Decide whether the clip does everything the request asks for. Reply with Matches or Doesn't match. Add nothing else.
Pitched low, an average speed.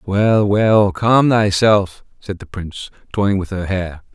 Matches